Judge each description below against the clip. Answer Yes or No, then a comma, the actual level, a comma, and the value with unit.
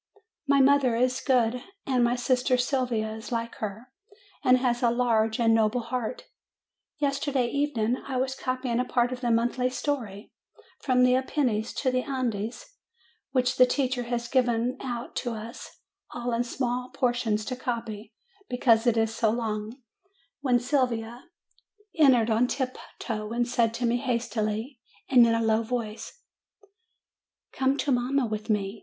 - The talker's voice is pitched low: No, high, 245 Hz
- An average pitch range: No, narrow, 2.0 semitones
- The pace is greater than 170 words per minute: No, average, 155 wpm